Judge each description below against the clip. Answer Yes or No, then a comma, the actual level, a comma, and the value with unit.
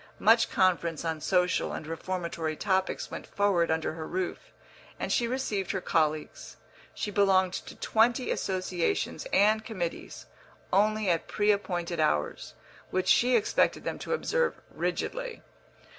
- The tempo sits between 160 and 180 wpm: No, slow, 135 wpm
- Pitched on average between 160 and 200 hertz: Yes, medium, 185 Hz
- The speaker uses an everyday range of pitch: Yes, average, 4.1 semitones